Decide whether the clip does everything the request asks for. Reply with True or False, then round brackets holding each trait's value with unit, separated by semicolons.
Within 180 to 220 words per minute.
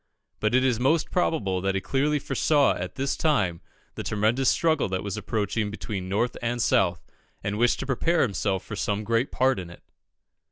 True (190 wpm)